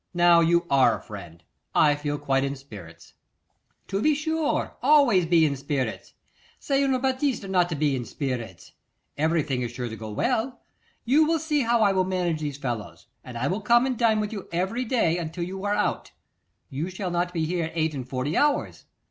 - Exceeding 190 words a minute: Yes, average, 200 wpm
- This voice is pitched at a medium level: Yes, medium, 170 Hz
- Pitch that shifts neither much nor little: No, wide, 8.2 semitones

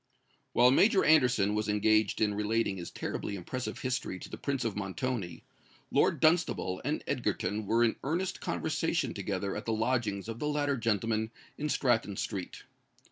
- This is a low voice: Yes, low, 115 Hz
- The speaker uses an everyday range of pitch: Yes, average, 4.1 semitones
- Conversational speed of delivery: Yes, average, 160 wpm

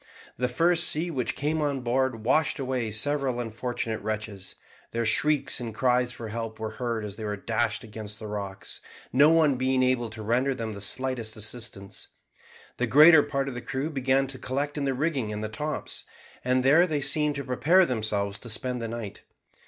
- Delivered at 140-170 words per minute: No, average, 190 wpm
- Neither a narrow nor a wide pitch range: Yes, average, 3.8 semitones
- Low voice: Yes, low, 125 Hz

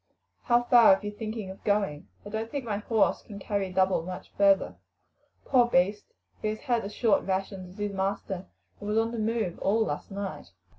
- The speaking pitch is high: Yes, high, 205 Hz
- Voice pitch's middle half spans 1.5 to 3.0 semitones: Yes, narrow, 2.6 semitones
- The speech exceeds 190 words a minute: Yes, average, 200 wpm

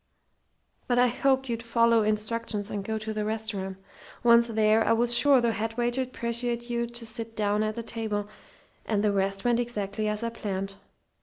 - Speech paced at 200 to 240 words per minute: No, average, 185 wpm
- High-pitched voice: Yes, high, 225 Hz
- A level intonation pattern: Yes, narrow, 2.0 semitones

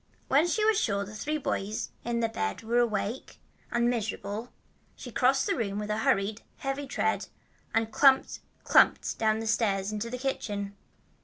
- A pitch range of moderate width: Yes, average, 3.5 semitones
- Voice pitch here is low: No, high, 225 Hz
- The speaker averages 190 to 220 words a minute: No, average, 170 wpm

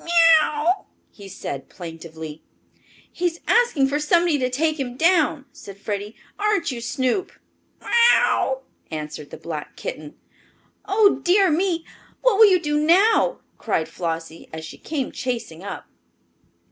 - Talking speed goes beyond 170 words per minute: No, average, 140 wpm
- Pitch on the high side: Yes, very high, 280 Hz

